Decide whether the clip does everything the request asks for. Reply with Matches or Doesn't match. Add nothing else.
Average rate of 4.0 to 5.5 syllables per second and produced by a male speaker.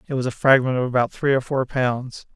Doesn't match